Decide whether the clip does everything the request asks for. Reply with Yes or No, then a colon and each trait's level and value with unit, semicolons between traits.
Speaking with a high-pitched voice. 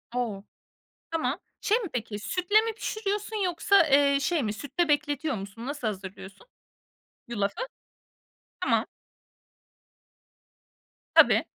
Yes: very high, 290 Hz